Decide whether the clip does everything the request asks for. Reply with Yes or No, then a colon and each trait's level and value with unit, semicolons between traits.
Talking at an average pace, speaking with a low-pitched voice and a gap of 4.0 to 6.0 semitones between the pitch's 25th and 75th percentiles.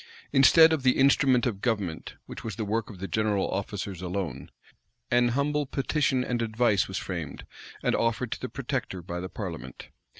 Yes: average, 175 wpm; low, 110 Hz; average, 5.1 semitones